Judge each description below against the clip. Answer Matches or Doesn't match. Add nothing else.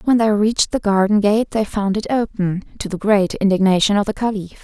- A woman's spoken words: Matches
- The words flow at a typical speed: Doesn't match